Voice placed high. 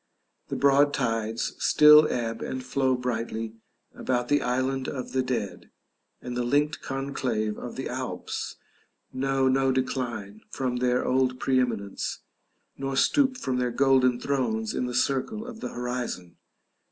No: low, 130 Hz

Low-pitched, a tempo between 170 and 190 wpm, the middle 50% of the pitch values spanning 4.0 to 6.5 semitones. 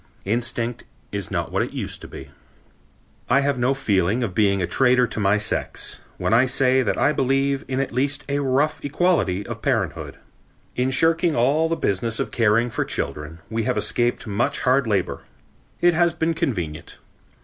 Yes: low, 125 Hz; average, 180 wpm; average, 4.8 semitones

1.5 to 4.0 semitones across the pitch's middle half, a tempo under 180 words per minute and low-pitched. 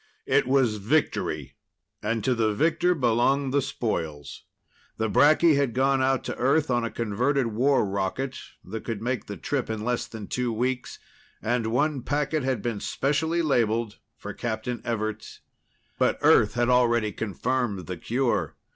Yes: average, 3.6 semitones; average, 155 wpm; low, 120 Hz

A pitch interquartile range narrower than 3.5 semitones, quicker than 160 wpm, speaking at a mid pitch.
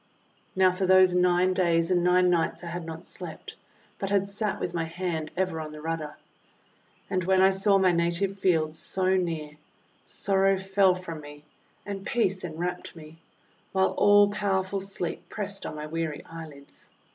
Yes: average, 2.7 semitones; average, 170 wpm; medium, 180 Hz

